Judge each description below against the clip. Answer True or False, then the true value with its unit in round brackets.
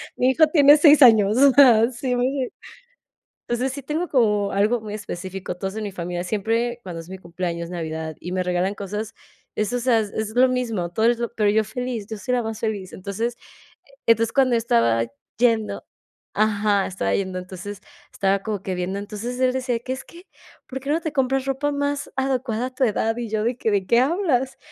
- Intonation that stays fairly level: False (4.5 semitones)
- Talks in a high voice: True (225 Hz)